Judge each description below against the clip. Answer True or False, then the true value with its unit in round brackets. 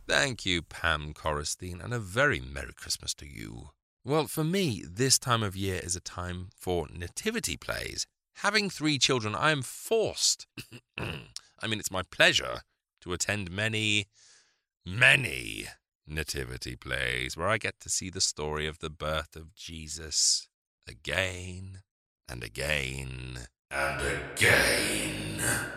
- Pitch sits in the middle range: False (90 Hz)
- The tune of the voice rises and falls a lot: True (6.6 semitones)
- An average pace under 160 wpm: True (135 wpm)